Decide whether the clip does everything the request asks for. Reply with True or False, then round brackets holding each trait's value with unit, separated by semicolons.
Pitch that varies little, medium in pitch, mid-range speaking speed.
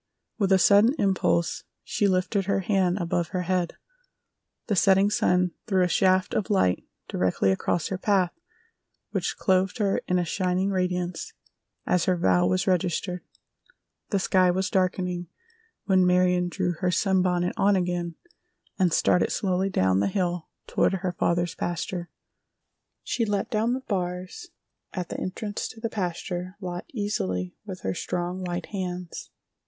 True (1.6 semitones; 180 Hz; 150 wpm)